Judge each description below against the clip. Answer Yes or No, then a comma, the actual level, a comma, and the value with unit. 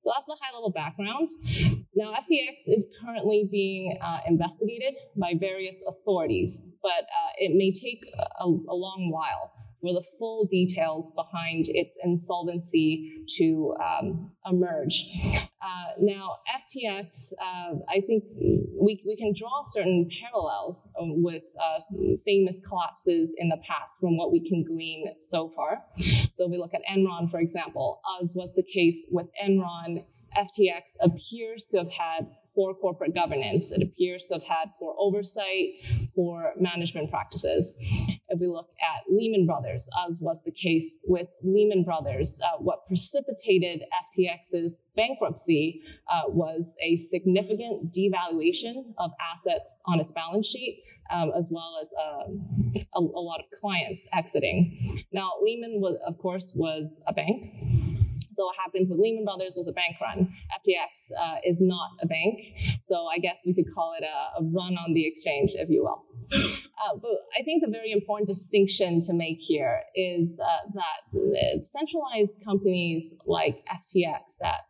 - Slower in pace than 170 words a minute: Yes, average, 155 wpm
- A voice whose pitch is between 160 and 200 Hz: Yes, medium, 185 Hz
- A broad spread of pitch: No, average, 3.9 semitones